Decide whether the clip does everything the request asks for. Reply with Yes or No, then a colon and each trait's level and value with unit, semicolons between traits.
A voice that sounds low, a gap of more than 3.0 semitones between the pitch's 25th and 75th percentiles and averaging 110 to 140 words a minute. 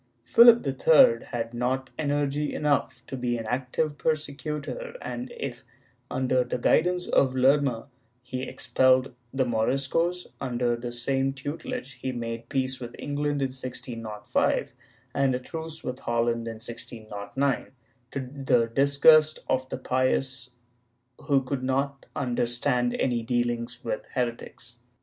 No: low, 130 Hz; average, 2.7 semitones; slow, 135 wpm